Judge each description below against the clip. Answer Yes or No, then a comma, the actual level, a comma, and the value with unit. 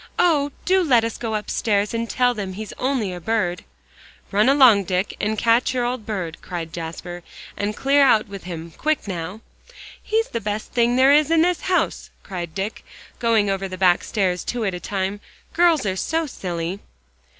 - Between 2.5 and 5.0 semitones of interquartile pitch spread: No, wide, 5.5 semitones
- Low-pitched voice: No, high, 215 Hz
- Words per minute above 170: Yes, average, 185 wpm